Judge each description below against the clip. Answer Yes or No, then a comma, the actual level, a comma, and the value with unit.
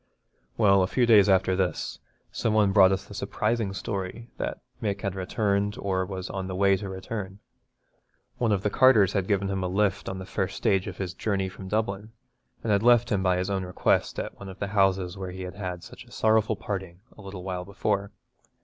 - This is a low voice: Yes, very low, 95 Hz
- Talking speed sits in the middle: No, fast, 215 wpm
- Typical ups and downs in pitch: No, narrow, 1.7 semitones